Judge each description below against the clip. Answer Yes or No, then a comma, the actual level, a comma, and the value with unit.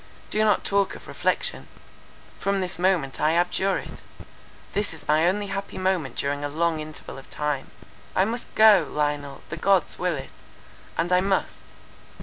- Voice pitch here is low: No, medium, 175 Hz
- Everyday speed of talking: Yes, average, 160 wpm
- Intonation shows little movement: No, average, 4.6 semitones